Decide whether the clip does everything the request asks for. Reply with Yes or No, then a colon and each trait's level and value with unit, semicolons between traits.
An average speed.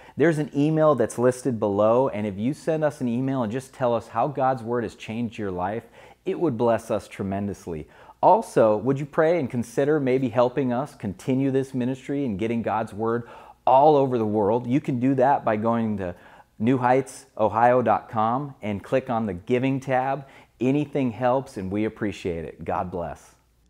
Yes: average, 180 wpm